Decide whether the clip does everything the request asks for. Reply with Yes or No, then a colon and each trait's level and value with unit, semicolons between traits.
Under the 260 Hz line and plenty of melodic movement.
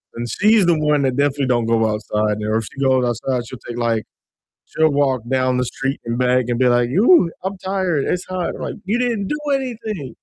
Yes: low, 135 Hz; wide, 7.3 semitones